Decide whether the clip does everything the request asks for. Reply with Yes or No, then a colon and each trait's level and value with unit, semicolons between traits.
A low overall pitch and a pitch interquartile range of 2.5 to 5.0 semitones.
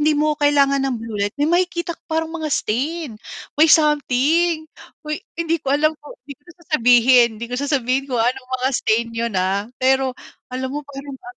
No: very high, 275 Hz; average, 3.7 semitones